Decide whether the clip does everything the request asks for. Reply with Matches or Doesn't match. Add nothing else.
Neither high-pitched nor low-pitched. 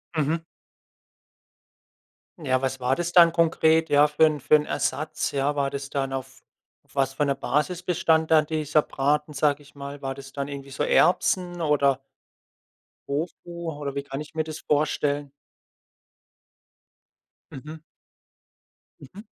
Matches